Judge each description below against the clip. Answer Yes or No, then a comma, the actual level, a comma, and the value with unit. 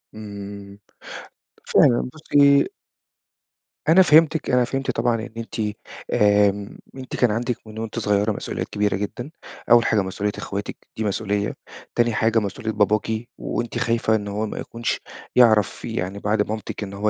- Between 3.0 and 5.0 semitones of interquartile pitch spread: No, narrow, 2.6 semitones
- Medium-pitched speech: No, low, 110 Hz